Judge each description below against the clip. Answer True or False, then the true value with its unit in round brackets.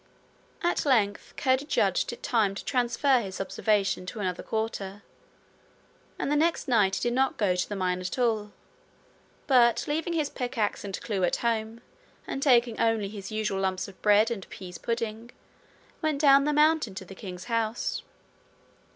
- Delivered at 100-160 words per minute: False (170 wpm)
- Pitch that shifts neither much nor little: True (4.6 semitones)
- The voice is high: True (220 Hz)